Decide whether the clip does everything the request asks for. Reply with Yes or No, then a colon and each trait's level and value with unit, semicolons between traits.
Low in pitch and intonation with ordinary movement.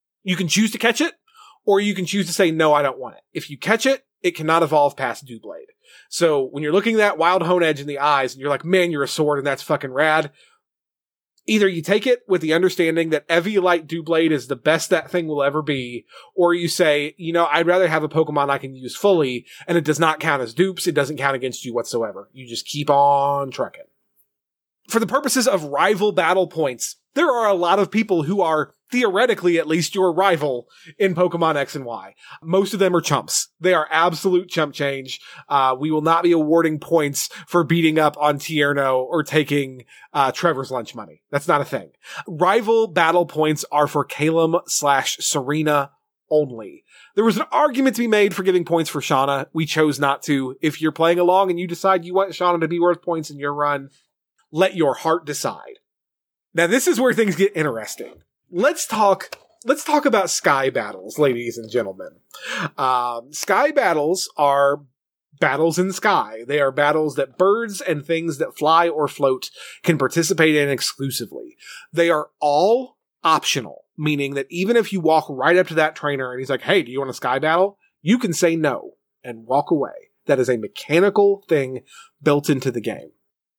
No: medium, 160 Hz; average, 4.6 semitones